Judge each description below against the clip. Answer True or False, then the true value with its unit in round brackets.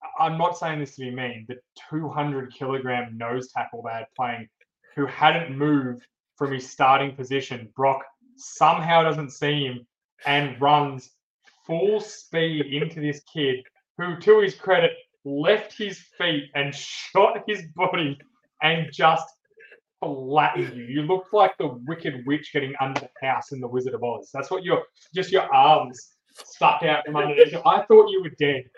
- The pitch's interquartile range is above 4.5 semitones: True (4.9 semitones)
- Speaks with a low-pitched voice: False (150 Hz)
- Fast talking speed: False (165 wpm)